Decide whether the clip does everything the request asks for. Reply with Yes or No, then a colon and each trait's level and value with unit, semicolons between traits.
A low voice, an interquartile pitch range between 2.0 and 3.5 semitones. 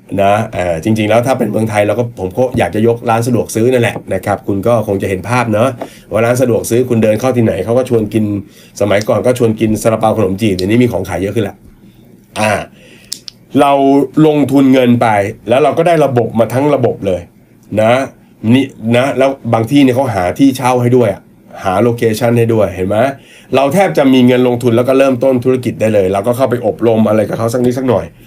Yes: low, 115 Hz; average, 3.0 semitones